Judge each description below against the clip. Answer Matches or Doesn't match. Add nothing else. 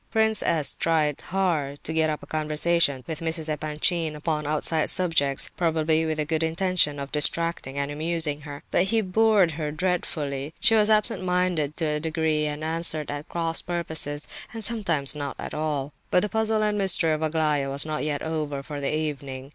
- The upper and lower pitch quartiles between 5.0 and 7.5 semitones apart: Doesn't match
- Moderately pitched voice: Matches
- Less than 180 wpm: Doesn't match